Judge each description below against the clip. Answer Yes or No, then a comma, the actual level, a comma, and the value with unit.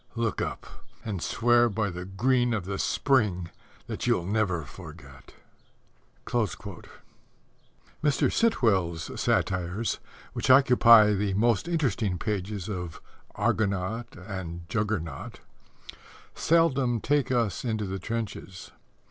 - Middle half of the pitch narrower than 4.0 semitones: No, average, 4.4 semitones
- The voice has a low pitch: Yes, low, 105 Hz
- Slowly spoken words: Yes, slow, 105 wpm